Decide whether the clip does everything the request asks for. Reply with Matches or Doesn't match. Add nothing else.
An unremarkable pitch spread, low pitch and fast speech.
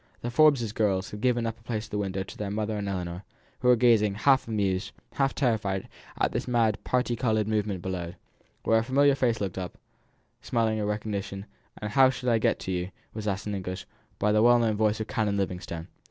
Matches